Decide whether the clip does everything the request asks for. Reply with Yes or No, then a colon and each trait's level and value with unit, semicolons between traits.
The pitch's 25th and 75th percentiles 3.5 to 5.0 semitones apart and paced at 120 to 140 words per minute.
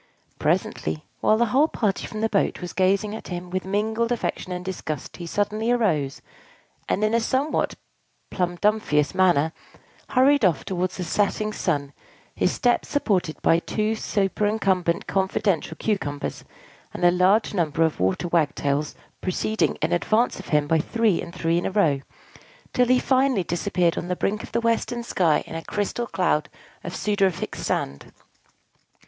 No: average, 4.4 semitones; average, 155 wpm